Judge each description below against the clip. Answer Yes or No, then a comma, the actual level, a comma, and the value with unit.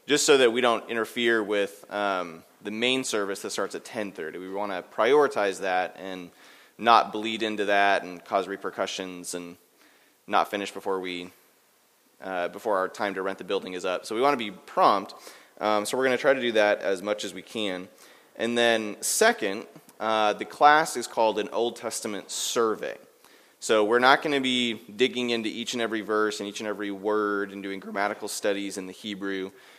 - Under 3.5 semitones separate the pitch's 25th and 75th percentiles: Yes, average, 2.7 semitones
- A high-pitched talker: No, low, 105 Hz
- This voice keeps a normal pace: No, fast, 210 wpm